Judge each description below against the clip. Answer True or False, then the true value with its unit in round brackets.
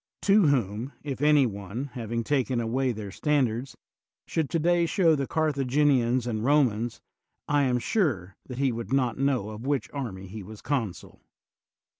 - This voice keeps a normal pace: True (160 wpm)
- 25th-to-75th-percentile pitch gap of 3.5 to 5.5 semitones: True (4.3 semitones)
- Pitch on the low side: True (130 Hz)